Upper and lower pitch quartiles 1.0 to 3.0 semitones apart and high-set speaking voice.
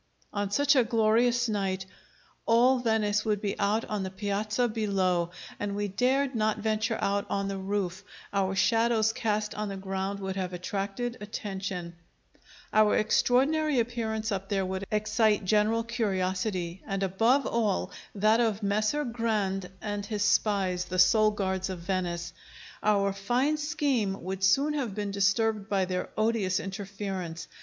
Yes: average, 2.7 semitones; high, 205 Hz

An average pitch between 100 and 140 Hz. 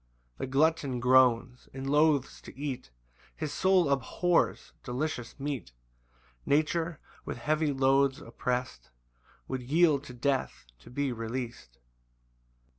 Yes: low, 135 Hz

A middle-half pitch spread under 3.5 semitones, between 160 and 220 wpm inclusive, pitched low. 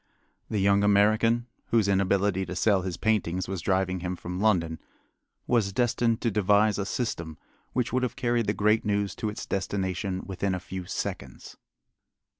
Yes: average, 2.8 semitones; average, 165 wpm; low, 100 Hz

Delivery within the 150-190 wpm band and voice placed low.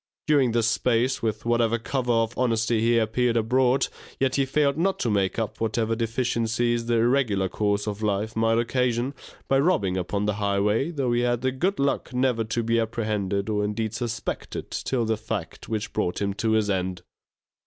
Yes: average, 185 wpm; low, 115 Hz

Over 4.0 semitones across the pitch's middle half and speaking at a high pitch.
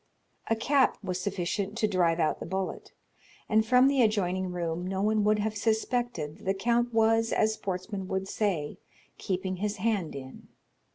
No: average, 3.2 semitones; high, 200 Hz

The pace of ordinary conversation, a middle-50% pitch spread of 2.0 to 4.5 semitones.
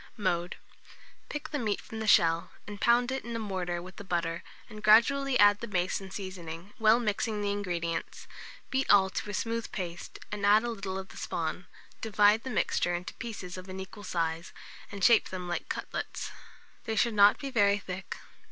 Yes: average, 195 wpm; average, 3.5 semitones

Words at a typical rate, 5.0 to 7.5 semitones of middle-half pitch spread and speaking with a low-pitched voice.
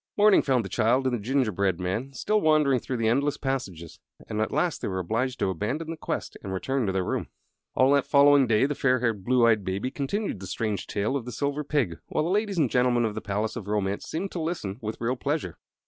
No: fast, 240 wpm; wide, 5.4 semitones; low, 125 Hz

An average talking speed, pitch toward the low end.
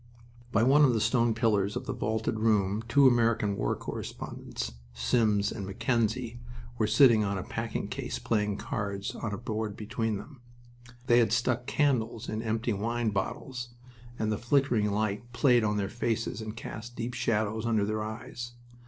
Yes: average, 170 wpm; low, 110 Hz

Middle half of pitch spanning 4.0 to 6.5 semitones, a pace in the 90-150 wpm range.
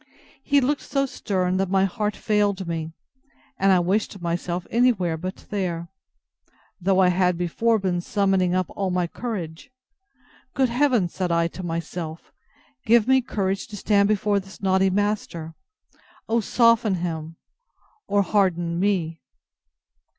No: average, 3.2 semitones; average, 145 wpm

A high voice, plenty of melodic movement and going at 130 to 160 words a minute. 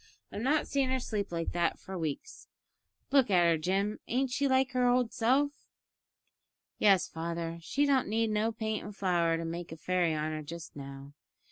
No: high, 195 Hz; wide, 6.9 semitones; average, 190 wpm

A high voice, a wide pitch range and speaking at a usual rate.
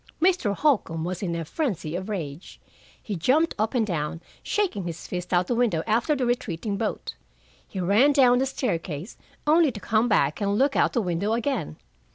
Yes: high, 210 Hz; wide, 6.5 semitones; average, 190 wpm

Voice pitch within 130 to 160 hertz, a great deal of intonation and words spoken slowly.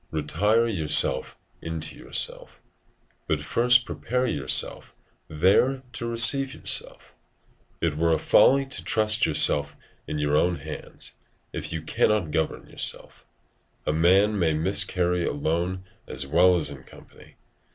No: very low, 85 Hz; wide, 5.8 semitones; slow, 130 wpm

